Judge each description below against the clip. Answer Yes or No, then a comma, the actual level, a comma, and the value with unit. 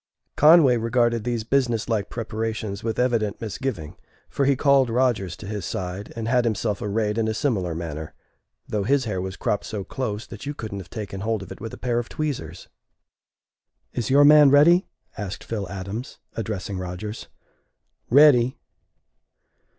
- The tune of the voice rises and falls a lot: No, average, 3.9 semitones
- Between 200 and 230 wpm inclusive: No, average, 165 wpm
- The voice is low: Yes, low, 110 Hz